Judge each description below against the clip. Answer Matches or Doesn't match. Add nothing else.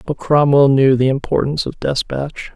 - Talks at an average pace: Matches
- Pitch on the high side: Doesn't match